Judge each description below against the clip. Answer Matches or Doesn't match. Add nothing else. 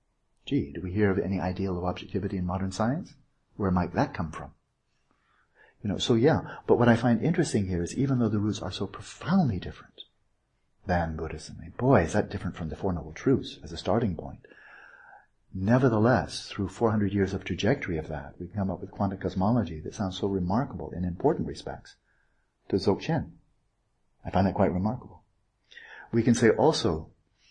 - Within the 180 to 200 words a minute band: Matches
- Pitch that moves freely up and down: Doesn't match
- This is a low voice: Matches